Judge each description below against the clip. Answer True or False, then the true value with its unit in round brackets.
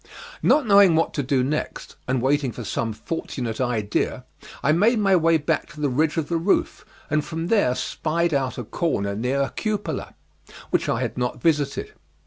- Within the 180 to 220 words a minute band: True (185 wpm)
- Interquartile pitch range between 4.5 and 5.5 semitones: True (4.9 semitones)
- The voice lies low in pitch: False (150 Hz)